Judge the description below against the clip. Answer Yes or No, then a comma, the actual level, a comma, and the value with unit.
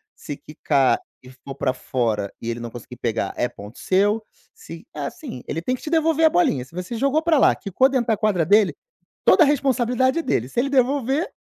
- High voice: Yes, high, 210 Hz